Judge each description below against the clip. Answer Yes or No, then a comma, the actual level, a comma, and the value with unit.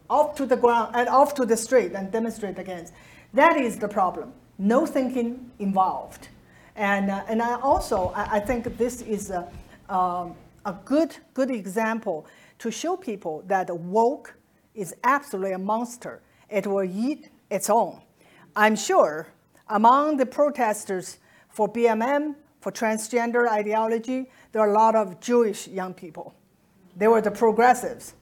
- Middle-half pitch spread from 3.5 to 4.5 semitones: Yes, average, 4.0 semitones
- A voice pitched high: Yes, high, 225 Hz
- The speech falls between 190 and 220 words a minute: No, average, 150 wpm